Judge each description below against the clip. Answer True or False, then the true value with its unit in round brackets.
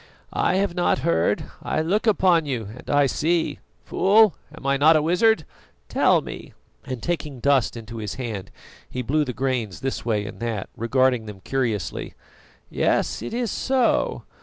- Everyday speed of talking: True (170 wpm)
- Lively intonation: True (6.6 semitones)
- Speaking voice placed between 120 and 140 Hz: True (135 Hz)